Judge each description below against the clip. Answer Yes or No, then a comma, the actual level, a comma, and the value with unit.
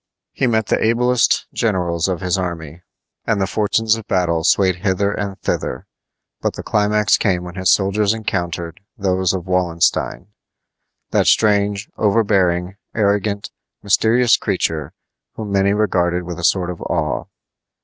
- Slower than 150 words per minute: Yes, average, 140 wpm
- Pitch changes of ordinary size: Yes, average, 3.0 semitones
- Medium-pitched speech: No, very low, 95 Hz